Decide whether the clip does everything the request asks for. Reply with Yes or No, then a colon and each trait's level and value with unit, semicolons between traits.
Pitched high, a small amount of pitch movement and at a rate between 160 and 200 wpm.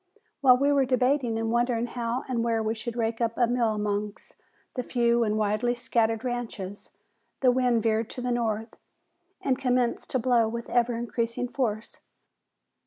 Yes: high, 235 Hz; narrow, 1.8 semitones; average, 170 wpm